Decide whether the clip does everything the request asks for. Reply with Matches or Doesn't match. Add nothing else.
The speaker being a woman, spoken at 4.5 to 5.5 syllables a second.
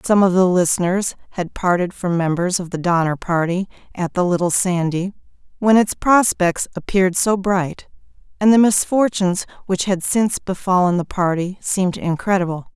Matches